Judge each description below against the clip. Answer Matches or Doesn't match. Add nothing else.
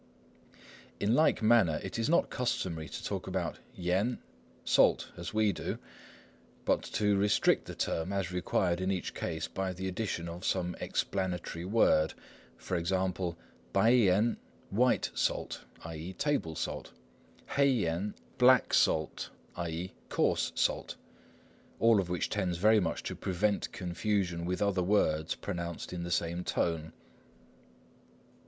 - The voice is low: Matches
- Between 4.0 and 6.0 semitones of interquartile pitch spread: Doesn't match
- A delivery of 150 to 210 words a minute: Doesn't match